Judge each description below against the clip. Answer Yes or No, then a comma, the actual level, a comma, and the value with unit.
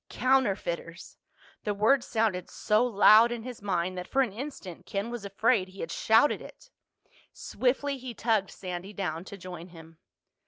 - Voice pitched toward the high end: Yes, high, 205 Hz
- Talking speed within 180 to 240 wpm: No, average, 160 wpm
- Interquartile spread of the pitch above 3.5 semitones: Yes, average, 4.7 semitones